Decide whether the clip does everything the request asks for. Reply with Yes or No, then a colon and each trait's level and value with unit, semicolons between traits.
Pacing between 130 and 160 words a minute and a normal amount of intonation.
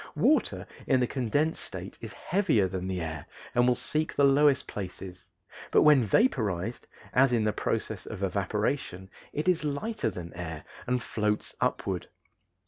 No: average, 155 wpm; wide, 7.2 semitones